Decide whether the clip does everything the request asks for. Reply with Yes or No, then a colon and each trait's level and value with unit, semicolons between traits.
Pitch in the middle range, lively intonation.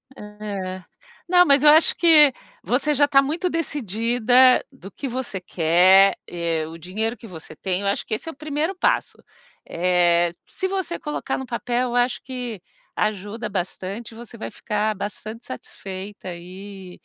No: high, 220 Hz; wide, 6.0 semitones